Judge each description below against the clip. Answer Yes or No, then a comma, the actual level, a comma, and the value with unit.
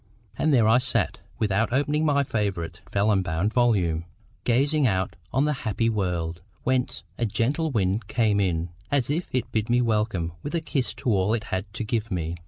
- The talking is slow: No, average, 190 wpm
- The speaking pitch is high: No, low, 110 Hz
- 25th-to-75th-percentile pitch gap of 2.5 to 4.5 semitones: No, average, 5.2 semitones